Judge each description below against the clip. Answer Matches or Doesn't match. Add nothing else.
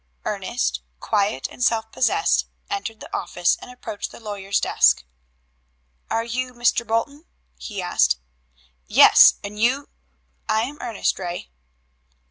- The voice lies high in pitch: Matches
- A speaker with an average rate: Doesn't match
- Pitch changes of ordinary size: Matches